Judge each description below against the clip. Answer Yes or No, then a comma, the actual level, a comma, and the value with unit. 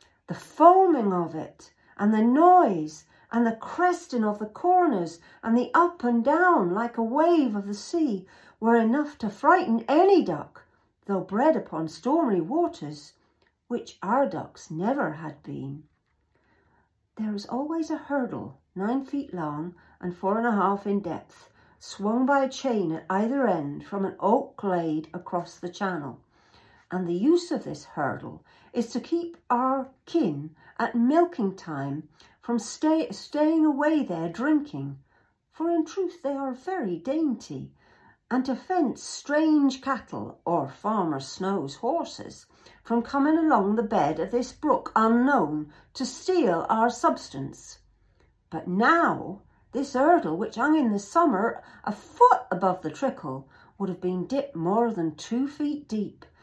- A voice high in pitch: Yes, high, 235 Hz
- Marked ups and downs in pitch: Yes, wide, 8.5 semitones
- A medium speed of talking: Yes, average, 150 wpm